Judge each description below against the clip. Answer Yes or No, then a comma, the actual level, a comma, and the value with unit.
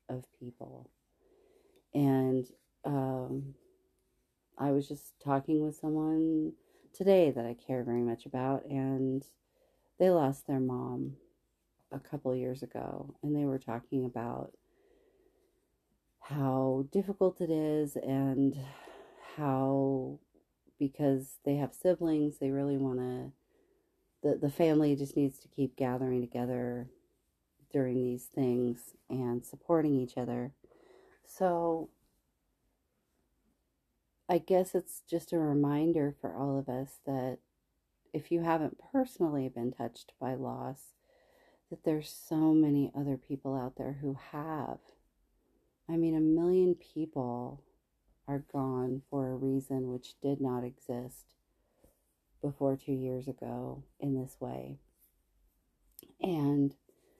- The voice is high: No, medium, 140 Hz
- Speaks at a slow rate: Yes, slow, 120 wpm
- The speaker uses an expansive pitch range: No, average, 3.7 semitones